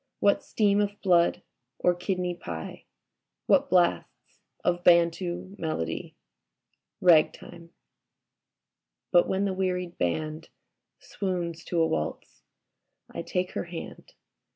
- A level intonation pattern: Yes, narrow, 1.8 semitones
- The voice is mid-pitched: Yes, medium, 175 Hz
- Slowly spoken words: Yes, slow, 105 wpm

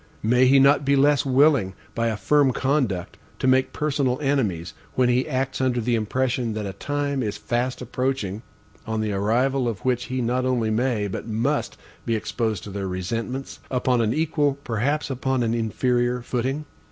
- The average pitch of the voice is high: No, low, 125 Hz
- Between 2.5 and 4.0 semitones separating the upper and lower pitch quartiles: Yes, average, 3.3 semitones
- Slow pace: No, average, 175 wpm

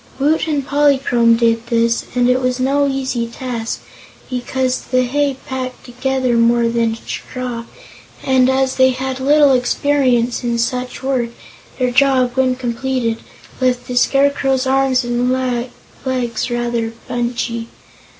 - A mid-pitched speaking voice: No, very high, 255 Hz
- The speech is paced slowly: Yes, slow, 130 wpm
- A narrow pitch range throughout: Yes, narrow, 1.7 semitones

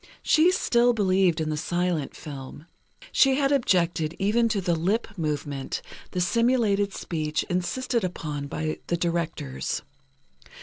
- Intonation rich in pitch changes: Yes, wide, 6.4 semitones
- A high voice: No, medium, 180 Hz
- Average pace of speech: No, slow, 130 wpm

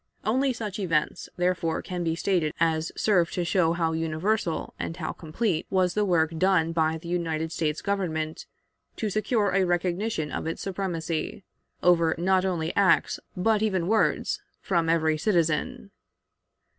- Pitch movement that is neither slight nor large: Yes, average, 3.2 semitones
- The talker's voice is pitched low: No, medium, 175 Hz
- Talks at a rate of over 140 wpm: Yes, average, 150 wpm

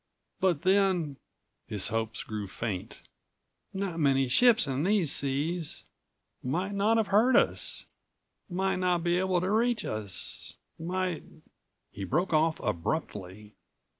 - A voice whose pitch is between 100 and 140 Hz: No, medium, 170 Hz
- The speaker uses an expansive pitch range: Yes, wide, 7.4 semitones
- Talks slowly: Yes, slow, 125 wpm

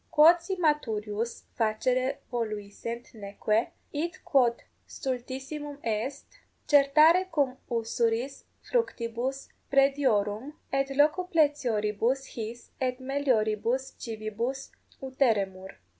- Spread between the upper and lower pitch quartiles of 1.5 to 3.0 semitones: No, average, 4.1 semitones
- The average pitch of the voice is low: No, very high, 255 Hz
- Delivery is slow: Yes, slow, 85 wpm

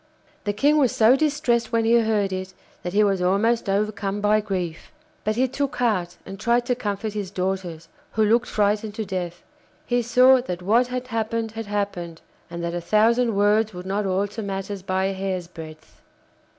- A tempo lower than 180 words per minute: No, average, 190 wpm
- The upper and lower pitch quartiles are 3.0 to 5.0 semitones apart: Yes, average, 3.4 semitones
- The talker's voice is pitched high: Yes, high, 205 Hz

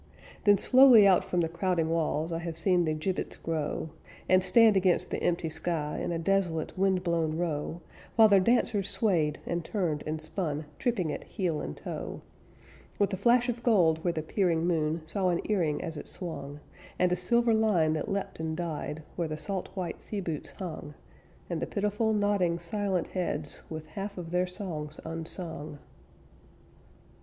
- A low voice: No, medium, 175 Hz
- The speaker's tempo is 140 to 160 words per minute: No, average, 175 wpm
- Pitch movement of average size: Yes, average, 3.6 semitones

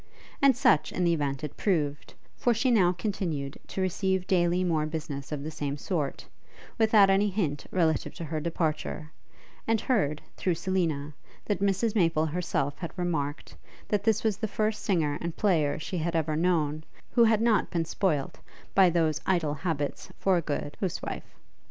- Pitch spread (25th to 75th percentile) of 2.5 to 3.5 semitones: No, average, 4.2 semitones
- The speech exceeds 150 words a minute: Yes, average, 170 wpm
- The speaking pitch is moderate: Yes, medium, 170 Hz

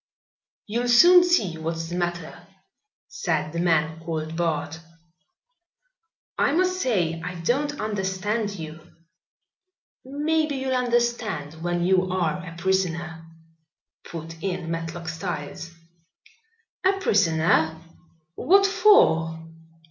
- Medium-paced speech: No, slow, 100 wpm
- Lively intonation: Yes, wide, 6.7 semitones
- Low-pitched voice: No, medium, 180 Hz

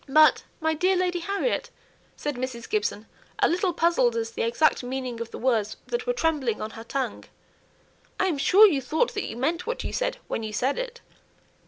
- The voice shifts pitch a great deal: Yes, wide, 7.6 semitones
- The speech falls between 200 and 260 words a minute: Yes, fast, 205 wpm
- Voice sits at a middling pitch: No, very high, 295 Hz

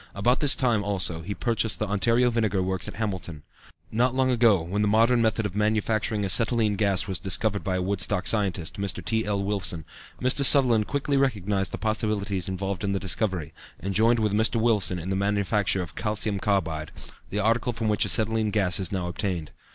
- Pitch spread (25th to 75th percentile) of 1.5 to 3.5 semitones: Yes, average, 2.8 semitones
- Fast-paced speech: No, average, 190 wpm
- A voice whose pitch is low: Yes, low, 105 Hz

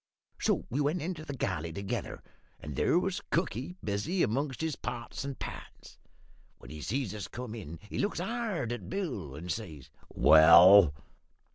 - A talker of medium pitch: No, low, 120 Hz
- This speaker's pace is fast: No, average, 165 wpm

